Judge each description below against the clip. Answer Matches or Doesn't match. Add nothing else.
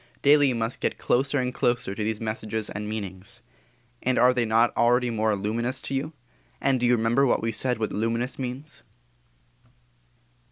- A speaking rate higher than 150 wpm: Matches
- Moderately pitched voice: Doesn't match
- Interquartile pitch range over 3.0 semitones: Doesn't match